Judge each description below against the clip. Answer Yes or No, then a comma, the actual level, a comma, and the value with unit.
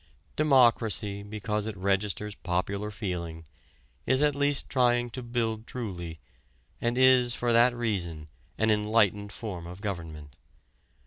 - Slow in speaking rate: Yes, slow, 125 wpm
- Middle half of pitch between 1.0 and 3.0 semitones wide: No, average, 4.1 semitones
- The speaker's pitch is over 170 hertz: No, low, 105 Hz